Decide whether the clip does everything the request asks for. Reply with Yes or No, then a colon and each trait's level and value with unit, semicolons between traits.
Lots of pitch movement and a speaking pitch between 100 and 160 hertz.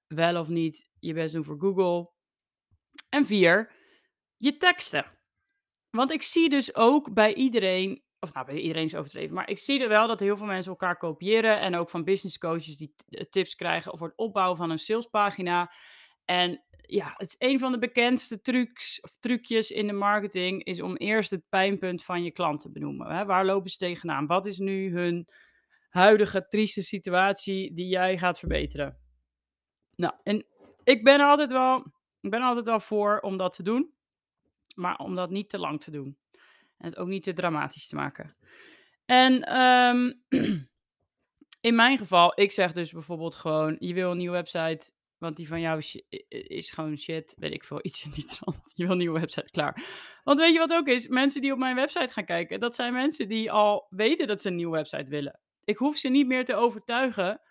No: wide, 6.3 semitones; high, 195 Hz